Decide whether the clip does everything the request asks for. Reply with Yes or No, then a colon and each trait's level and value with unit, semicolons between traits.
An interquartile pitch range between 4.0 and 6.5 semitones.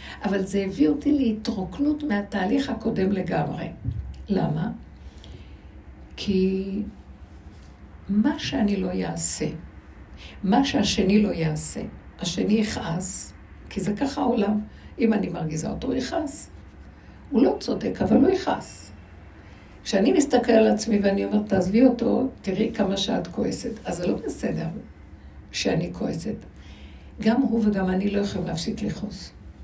Yes: average, 4.6 semitones